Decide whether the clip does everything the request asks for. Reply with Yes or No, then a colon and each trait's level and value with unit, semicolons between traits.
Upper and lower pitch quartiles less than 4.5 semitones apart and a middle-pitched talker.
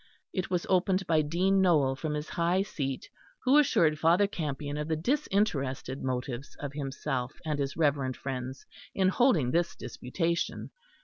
No: average, 5.1 semitones; medium, 155 Hz